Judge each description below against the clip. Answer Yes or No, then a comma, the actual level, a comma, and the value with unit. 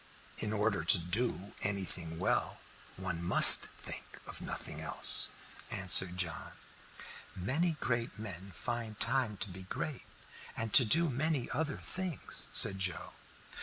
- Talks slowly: Yes, slow, 130 wpm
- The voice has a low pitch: Yes, low, 105 Hz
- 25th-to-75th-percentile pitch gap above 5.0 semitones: Yes, wide, 5.5 semitones